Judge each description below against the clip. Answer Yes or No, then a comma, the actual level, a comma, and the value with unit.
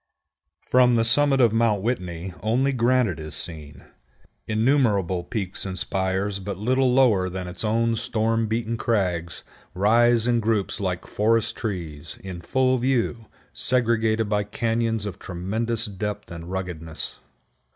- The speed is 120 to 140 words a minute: Yes, slow, 135 wpm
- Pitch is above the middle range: No, low, 110 Hz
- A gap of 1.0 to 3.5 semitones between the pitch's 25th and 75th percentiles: No, average, 3.9 semitones